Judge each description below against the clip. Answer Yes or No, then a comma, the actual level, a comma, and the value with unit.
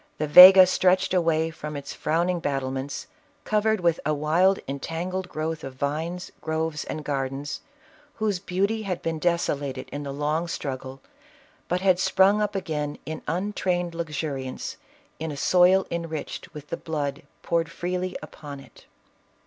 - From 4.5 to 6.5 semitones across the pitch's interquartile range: No, average, 3.8 semitones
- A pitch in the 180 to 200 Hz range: No, medium, 160 Hz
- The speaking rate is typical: Yes, average, 150 wpm